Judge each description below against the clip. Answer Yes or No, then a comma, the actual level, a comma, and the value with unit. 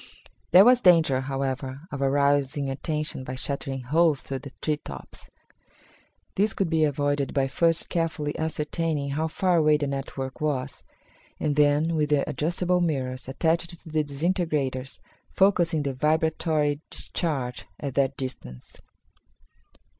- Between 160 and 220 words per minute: No, slow, 135 wpm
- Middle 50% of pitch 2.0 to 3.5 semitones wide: Yes, average, 3.0 semitones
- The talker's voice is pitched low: No, medium, 150 Hz